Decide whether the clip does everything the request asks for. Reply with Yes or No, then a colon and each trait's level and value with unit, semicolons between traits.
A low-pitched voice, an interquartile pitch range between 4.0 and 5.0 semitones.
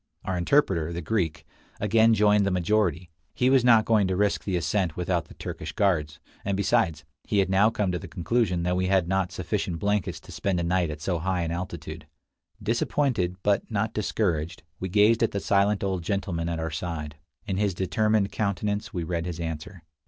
No: very low, 95 Hz; average, 3.4 semitones